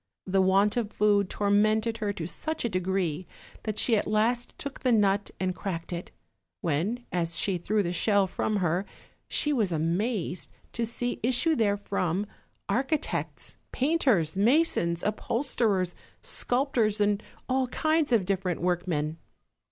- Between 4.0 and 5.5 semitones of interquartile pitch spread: Yes, average, 4.5 semitones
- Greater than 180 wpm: No, average, 140 wpm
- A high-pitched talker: Yes, high, 205 Hz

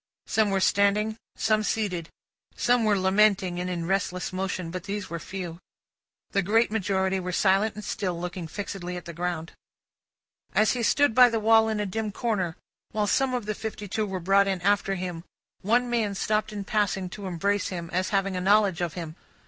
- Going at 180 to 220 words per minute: Yes, average, 195 wpm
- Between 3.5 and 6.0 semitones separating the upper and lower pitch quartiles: No, average, 2.8 semitones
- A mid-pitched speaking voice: No, high, 195 Hz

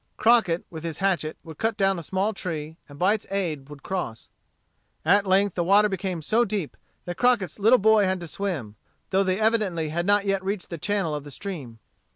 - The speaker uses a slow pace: No, fast, 205 wpm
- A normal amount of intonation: Yes, average, 3.8 semitones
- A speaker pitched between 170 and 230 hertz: Yes, high, 190 Hz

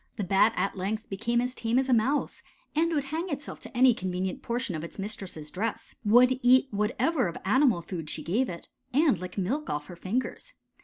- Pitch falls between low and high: No, high, 225 Hz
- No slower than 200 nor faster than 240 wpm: Yes, fast, 205 wpm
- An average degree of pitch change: No, wide, 5.7 semitones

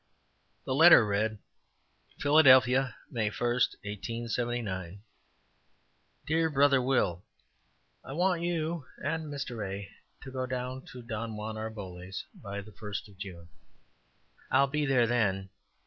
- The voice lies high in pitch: No, low, 120 Hz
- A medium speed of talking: No, slow, 125 wpm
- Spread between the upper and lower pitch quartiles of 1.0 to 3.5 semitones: No, average, 4.9 semitones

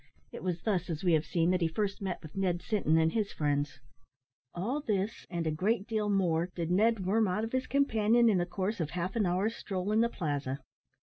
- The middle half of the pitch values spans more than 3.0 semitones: Yes, average, 4.2 semitones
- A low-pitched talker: No, medium, 185 Hz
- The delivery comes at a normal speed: No, fast, 230 wpm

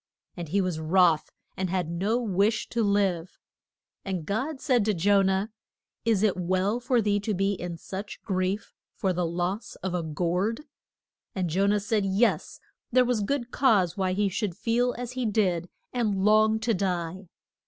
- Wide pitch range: No, average, 3.3 semitones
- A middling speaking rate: Yes, average, 175 wpm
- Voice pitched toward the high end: Yes, high, 195 Hz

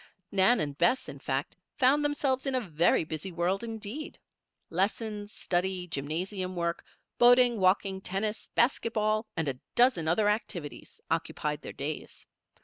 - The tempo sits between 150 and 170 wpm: No, average, 140 wpm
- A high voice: Yes, high, 195 Hz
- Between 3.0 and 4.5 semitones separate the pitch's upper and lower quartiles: No, average, 5.3 semitones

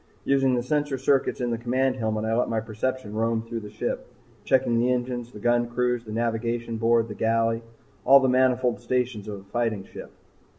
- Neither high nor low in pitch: No, low, 120 Hz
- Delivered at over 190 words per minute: Yes, average, 200 wpm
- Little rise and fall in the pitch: Yes, narrow, 2.0 semitones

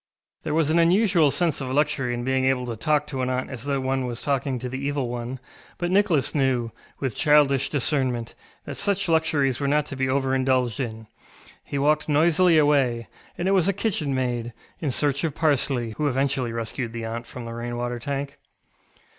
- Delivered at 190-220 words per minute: Yes, average, 200 wpm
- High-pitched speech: No, low, 135 Hz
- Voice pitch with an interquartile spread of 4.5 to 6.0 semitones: No, average, 3.3 semitones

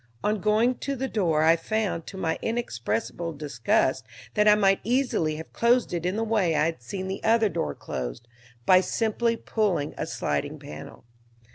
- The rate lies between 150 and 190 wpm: Yes, average, 175 wpm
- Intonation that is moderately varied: No, wide, 6.3 semitones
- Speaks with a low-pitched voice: No, high, 190 Hz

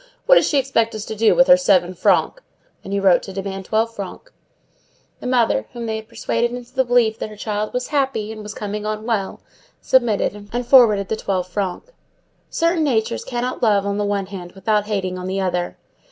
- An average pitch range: Yes, average, 3.5 semitones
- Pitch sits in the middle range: No, high, 215 Hz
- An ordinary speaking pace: No, fast, 210 wpm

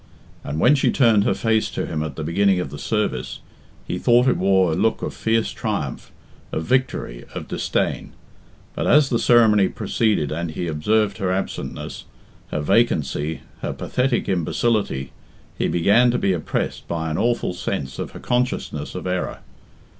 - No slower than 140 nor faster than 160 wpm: No, average, 170 wpm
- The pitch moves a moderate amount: No, wide, 6.4 semitones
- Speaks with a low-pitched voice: Yes, very low, 95 Hz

